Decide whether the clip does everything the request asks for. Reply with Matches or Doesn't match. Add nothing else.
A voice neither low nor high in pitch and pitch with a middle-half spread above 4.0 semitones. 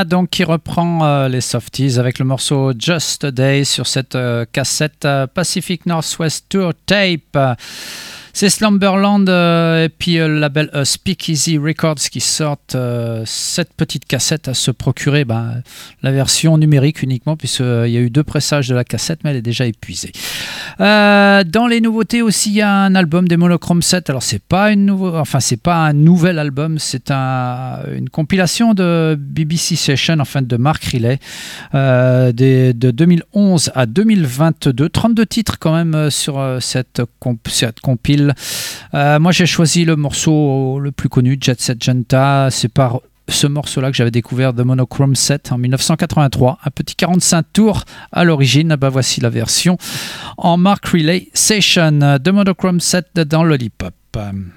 Matches